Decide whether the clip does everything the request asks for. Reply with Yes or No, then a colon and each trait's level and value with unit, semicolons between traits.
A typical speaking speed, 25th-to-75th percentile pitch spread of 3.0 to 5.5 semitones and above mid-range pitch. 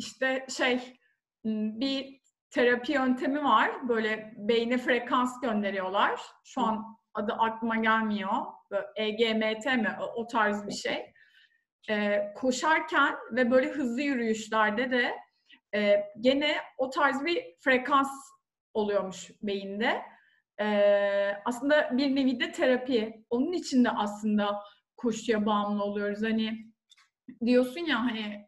Yes: average, 115 wpm; average, 3.7 semitones; high, 230 Hz